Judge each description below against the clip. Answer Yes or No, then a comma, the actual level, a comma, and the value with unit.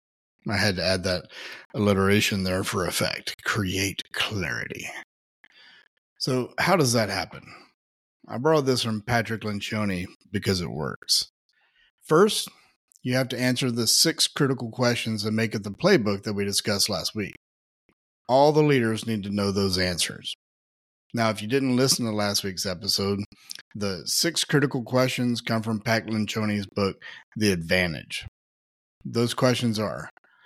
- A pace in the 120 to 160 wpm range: Yes, average, 150 wpm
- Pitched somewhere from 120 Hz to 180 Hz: No, low, 110 Hz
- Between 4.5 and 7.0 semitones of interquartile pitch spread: No, average, 3.8 semitones